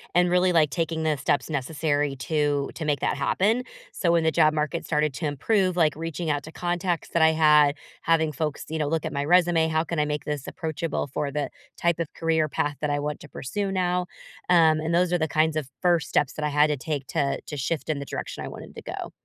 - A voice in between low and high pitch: Yes, medium, 155 Hz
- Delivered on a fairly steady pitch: Yes, narrow, 2.3 semitones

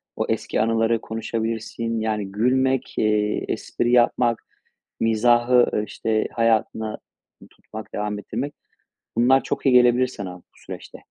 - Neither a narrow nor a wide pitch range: No, narrow, 2.0 semitones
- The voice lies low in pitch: Yes, low, 115 Hz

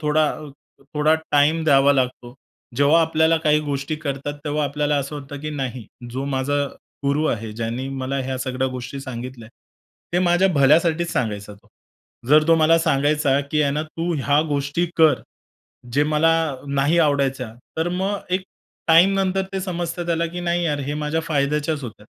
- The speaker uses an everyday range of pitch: Yes, average, 3.1 semitones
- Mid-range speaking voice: Yes, medium, 150 Hz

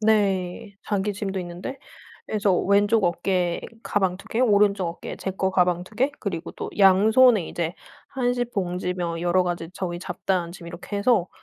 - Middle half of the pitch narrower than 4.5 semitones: Yes, average, 2.8 semitones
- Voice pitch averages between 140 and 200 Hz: Yes, high, 190 Hz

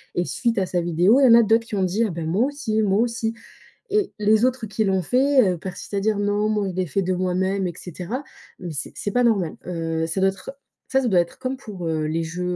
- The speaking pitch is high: Yes, high, 195 Hz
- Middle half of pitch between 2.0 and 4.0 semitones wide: No, average, 4.4 semitones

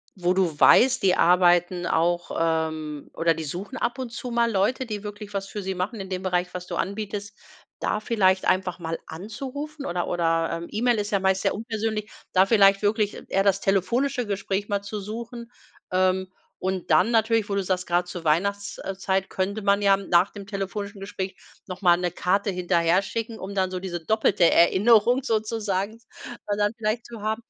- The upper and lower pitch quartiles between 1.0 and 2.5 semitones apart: No, average, 2.9 semitones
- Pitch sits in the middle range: No, high, 195 Hz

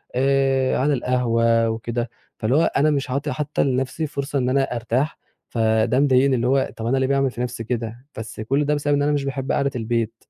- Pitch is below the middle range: Yes, low, 130 Hz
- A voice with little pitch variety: No, average, 3.0 semitones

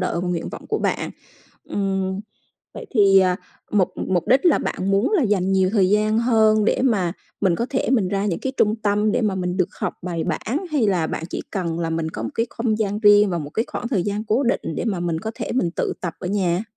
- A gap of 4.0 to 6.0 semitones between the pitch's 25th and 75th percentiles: No, average, 3.4 semitones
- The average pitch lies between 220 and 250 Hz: No, high, 200 Hz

